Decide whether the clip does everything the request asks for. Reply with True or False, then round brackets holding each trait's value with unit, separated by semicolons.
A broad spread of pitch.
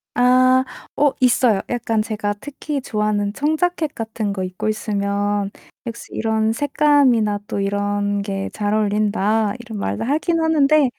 False (4.2 semitones)